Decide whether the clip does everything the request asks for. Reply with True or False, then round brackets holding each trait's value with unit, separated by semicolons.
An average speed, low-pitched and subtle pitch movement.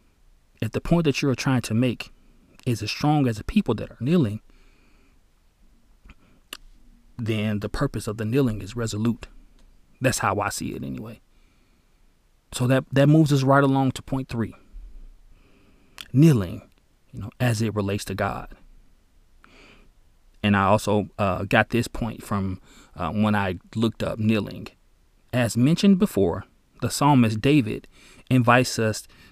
False (145 wpm; 110 Hz; 4.5 semitones)